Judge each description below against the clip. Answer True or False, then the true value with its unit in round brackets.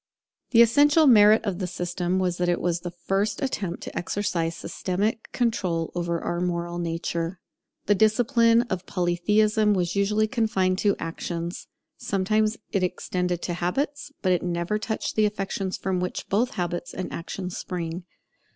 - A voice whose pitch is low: False (185 Hz)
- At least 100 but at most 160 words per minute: True (155 wpm)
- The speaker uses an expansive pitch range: False (3.5 semitones)